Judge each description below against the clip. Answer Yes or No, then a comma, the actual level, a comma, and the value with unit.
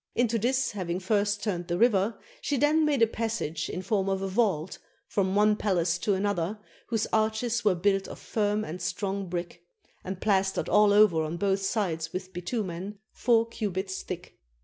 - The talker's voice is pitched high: Yes, high, 200 Hz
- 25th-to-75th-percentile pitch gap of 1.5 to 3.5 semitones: Yes, average, 3.0 semitones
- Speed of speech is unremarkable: Yes, average, 175 wpm